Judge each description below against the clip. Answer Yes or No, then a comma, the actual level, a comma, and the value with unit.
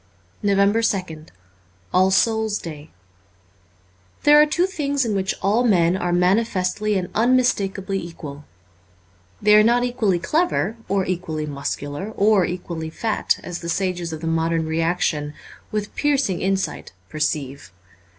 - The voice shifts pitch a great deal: No, average, 4.8 semitones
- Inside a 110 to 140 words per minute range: Yes, slow, 135 wpm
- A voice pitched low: No, high, 190 Hz